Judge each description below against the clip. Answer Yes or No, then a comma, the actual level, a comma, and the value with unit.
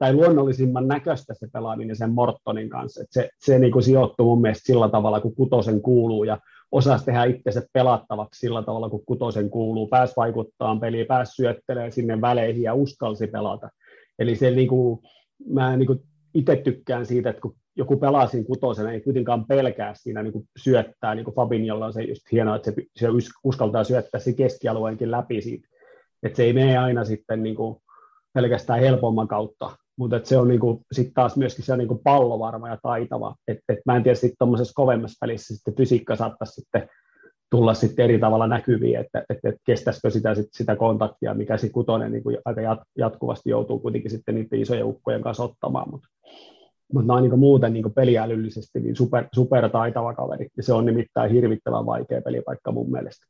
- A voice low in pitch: Yes, low, 120 Hz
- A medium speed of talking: No, fast, 185 wpm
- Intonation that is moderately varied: No, narrow, 2.3 semitones